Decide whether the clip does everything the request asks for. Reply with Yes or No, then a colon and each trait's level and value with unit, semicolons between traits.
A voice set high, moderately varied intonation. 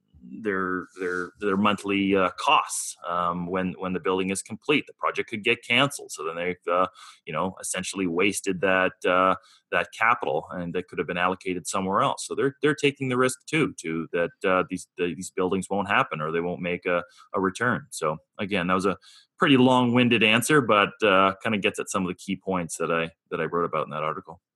No: very low, 95 Hz; average, 3.7 semitones